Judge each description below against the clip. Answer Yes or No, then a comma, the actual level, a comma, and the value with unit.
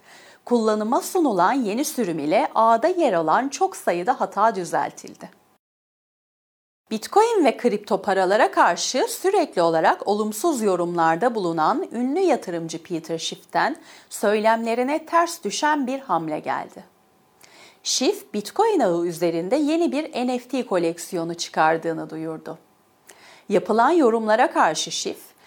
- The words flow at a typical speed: Yes, average, 110 wpm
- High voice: Yes, high, 220 Hz